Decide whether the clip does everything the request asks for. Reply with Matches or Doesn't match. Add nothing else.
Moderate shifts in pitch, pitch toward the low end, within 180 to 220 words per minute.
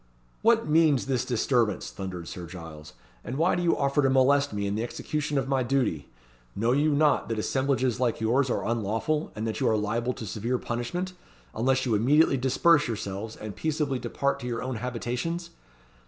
Matches